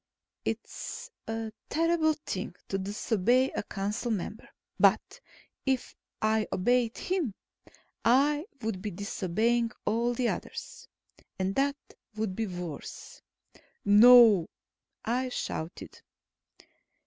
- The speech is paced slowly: Yes, slow, 100 wpm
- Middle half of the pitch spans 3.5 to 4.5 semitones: Yes, average, 4.2 semitones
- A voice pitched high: Yes, high, 225 Hz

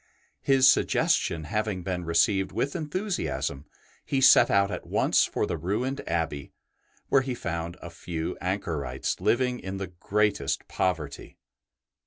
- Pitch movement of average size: No, wide, 6.8 semitones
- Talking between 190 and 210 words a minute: No, average, 140 wpm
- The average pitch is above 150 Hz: No, very low, 95 Hz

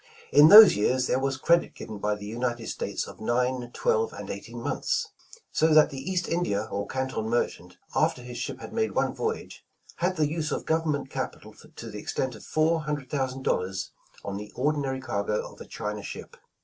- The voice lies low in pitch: Yes, low, 130 Hz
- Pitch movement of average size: No, wide, 6.3 semitones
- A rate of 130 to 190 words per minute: No, average, 200 wpm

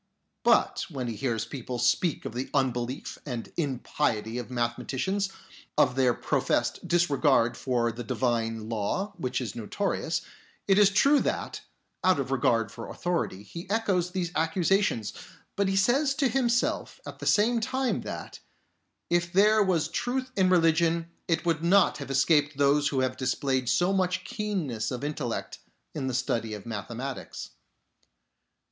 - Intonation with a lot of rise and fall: Yes, wide, 7.3 semitones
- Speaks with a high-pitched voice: No, medium, 145 Hz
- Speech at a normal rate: Yes, average, 150 wpm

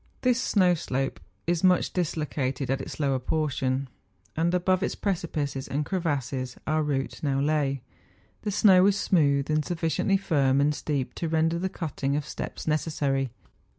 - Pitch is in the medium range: Yes, medium, 150 Hz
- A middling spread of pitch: Yes, average, 4.1 semitones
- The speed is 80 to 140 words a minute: No, average, 160 wpm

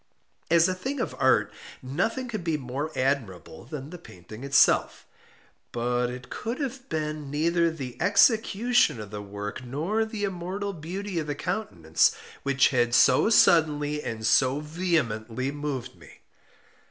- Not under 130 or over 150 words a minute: Yes, average, 145 wpm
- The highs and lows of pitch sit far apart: Yes, wide, 6.7 semitones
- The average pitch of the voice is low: No, medium, 150 Hz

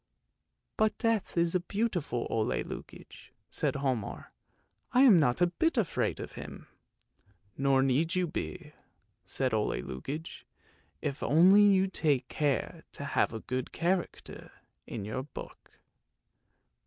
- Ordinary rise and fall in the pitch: No, wide, 6.6 semitones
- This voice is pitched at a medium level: Yes, medium, 150 Hz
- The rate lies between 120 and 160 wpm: Yes, average, 140 wpm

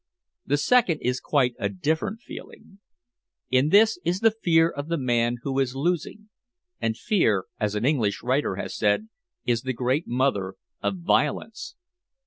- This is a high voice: No, medium, 140 Hz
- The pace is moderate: Yes, average, 155 wpm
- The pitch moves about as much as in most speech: No, wide, 6.5 semitones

